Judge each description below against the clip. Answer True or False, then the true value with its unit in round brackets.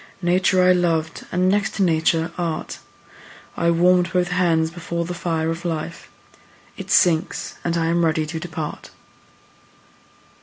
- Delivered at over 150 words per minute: False (145 wpm)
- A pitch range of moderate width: False (1.7 semitones)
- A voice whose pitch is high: False (170 Hz)